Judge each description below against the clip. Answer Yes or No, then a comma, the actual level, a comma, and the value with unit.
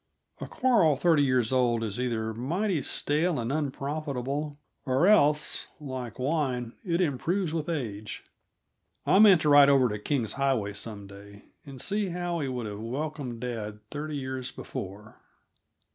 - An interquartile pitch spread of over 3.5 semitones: Yes, average, 4.8 semitones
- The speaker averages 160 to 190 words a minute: No, average, 150 wpm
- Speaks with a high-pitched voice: No, low, 135 Hz